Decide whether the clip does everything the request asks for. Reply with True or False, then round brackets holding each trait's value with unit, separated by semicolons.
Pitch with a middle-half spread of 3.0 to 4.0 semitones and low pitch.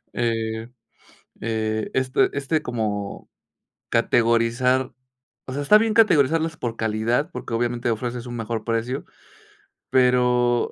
False (2.4 semitones; 120 Hz)